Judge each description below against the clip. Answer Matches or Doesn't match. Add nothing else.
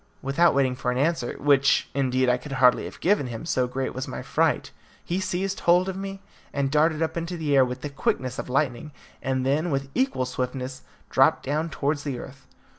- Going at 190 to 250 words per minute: Matches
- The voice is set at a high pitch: Doesn't match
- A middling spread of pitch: Matches